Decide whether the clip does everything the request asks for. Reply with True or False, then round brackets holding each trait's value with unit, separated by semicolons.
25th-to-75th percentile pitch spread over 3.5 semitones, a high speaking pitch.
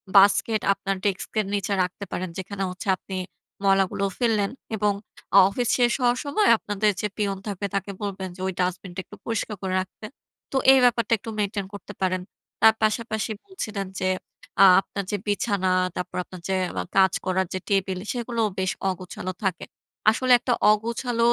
False (2.7 semitones; 200 Hz)